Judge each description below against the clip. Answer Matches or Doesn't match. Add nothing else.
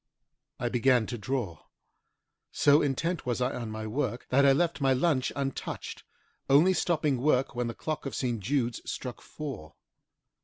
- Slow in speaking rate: Doesn't match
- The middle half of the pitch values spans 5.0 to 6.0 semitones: Doesn't match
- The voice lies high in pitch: Doesn't match